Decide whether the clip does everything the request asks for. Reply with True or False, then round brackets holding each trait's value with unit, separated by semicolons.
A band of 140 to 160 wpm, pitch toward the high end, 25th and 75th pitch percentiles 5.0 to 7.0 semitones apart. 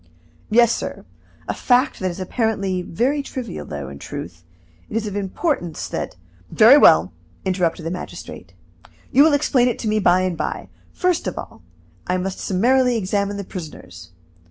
False (170 wpm; 200 Hz; 5.5 semitones)